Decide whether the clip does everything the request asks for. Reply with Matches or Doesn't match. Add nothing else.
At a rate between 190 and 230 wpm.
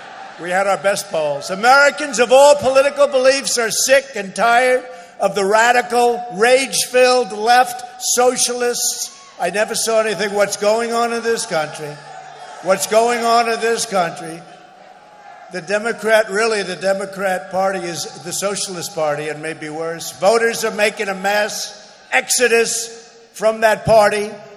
Doesn't match